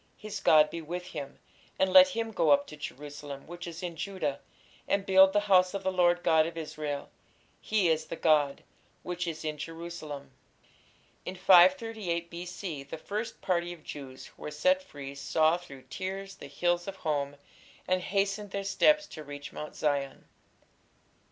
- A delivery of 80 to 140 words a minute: No, average, 170 wpm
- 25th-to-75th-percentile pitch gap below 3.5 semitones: No, average, 4.2 semitones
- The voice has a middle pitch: Yes, medium, 170 Hz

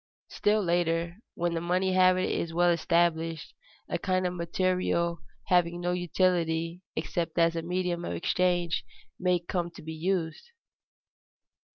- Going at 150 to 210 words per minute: No, average, 140 wpm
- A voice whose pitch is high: No, medium, 175 Hz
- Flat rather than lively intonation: Yes, narrow, 1.4 semitones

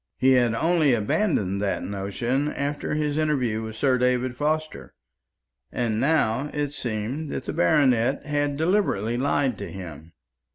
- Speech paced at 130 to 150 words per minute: Yes, average, 140 wpm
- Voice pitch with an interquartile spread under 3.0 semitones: No, average, 5.1 semitones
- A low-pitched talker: Yes, low, 130 Hz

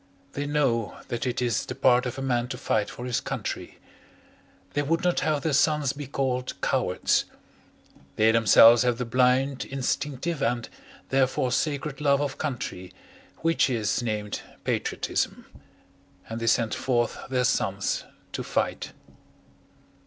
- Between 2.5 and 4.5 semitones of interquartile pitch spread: Yes, average, 3.2 semitones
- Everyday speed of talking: Yes, average, 145 wpm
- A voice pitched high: No, low, 125 Hz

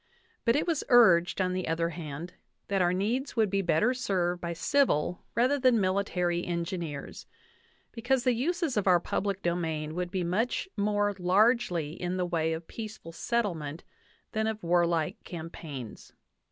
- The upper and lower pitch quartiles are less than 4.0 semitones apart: No, average, 4.6 semitones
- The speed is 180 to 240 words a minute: No, average, 165 wpm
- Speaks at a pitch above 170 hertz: Yes, medium, 185 Hz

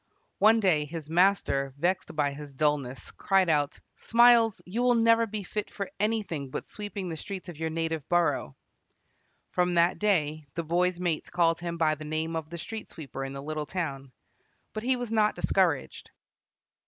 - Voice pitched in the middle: Yes, medium, 170 Hz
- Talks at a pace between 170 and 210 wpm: Yes, average, 180 wpm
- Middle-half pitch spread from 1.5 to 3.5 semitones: No, average, 4.8 semitones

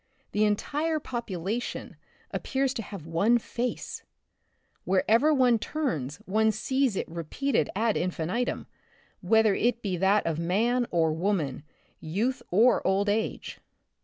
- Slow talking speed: Yes, slow, 130 wpm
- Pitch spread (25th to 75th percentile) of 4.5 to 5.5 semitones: Yes, average, 5.2 semitones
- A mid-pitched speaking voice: No, high, 215 Hz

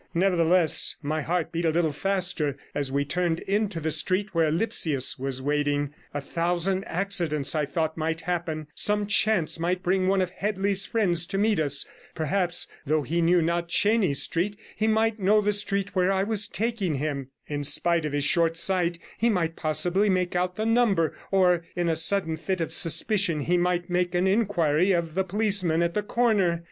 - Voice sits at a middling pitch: Yes, medium, 175 Hz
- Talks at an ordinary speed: Yes, average, 185 wpm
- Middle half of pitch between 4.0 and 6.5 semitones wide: No, average, 3.6 semitones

